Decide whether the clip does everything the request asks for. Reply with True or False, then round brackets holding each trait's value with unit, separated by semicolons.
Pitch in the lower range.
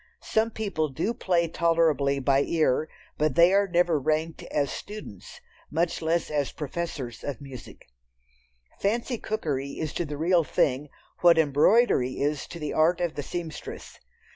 False (160 Hz)